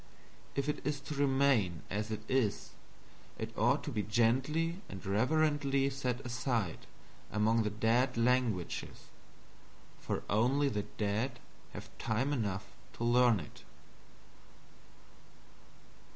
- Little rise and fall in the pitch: No, average, 4.4 semitones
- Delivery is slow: Yes, slow, 110 wpm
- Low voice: Yes, low, 120 Hz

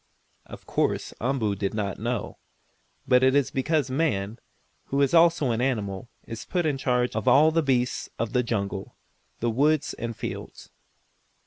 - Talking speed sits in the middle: Yes, average, 160 wpm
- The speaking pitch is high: No, low, 125 Hz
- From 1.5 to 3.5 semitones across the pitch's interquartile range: No, average, 4.1 semitones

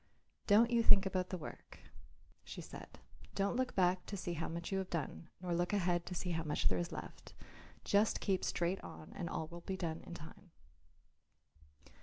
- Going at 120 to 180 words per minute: No, average, 195 wpm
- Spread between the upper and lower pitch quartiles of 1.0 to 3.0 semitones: Yes, narrow, 2.5 semitones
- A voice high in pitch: No, medium, 180 Hz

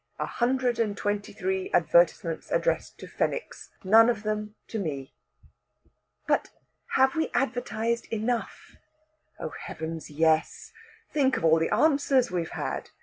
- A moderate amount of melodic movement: No, wide, 6.7 semitones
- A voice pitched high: Yes, high, 215 Hz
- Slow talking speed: Yes, slow, 130 wpm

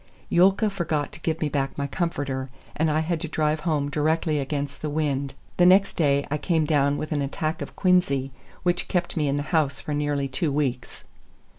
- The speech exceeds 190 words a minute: Yes, average, 200 wpm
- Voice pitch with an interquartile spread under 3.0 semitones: Yes, narrow, 2.5 semitones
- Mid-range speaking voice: Yes, medium, 150 Hz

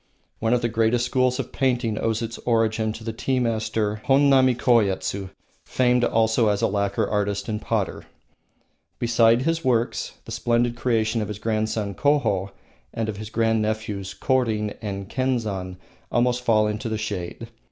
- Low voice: Yes, low, 115 Hz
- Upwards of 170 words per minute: No, average, 160 wpm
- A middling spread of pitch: No, narrow, 2.3 semitones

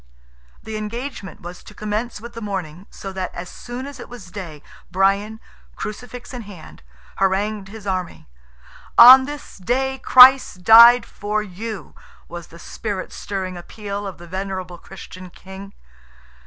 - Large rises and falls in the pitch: No, average, 3.9 semitones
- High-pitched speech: Yes, high, 205 Hz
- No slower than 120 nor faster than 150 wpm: Yes, average, 145 wpm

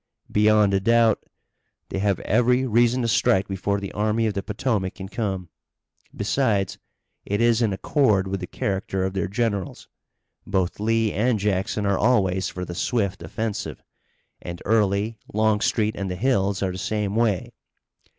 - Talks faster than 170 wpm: No, average, 160 wpm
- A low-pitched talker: Yes, low, 105 Hz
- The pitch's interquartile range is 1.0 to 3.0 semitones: Yes, average, 2.7 semitones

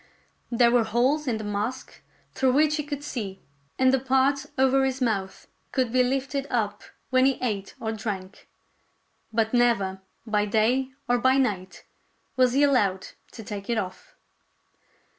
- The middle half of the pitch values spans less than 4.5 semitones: Yes, average, 4.0 semitones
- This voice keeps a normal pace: Yes, average, 160 wpm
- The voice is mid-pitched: No, high, 245 Hz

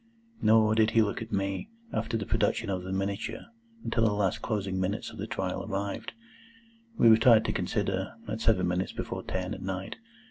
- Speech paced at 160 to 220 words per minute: Yes, average, 185 wpm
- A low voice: Yes, low, 100 Hz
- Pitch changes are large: No, average, 2.7 semitones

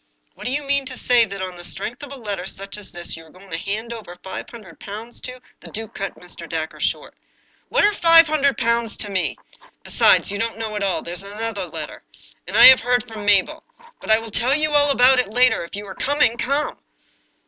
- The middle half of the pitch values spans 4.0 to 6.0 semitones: Yes, average, 4.6 semitones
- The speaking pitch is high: Yes, high, 225 Hz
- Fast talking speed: Yes, fast, 240 wpm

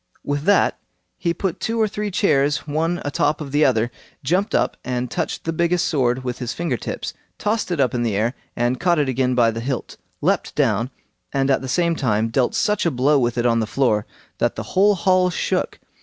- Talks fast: Yes, fast, 220 wpm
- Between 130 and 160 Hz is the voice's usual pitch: Yes, medium, 140 Hz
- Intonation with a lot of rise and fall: Yes, wide, 5.8 semitones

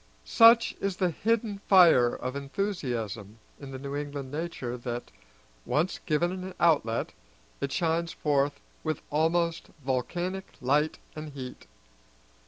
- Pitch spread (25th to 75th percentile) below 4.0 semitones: No, average, 4.8 semitones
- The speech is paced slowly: Yes, slow, 125 wpm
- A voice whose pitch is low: No, medium, 150 Hz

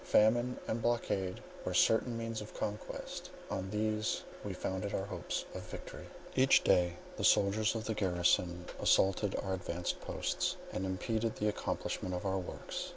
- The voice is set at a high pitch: No, low, 105 Hz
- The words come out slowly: No, average, 160 wpm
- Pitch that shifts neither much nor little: Yes, average, 3.0 semitones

